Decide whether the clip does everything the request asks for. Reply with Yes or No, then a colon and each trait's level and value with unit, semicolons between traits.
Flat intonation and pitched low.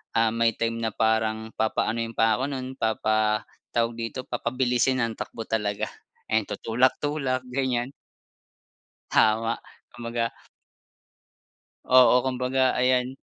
Yes: narrow, 2.3 semitones; low, 115 Hz